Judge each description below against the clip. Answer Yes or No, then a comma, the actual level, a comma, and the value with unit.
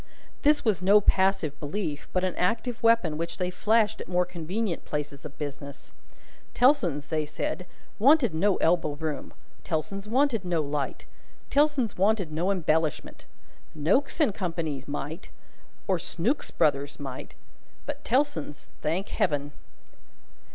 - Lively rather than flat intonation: Yes, wide, 6.0 semitones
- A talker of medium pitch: Yes, medium, 180 Hz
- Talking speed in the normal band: No, slow, 130 wpm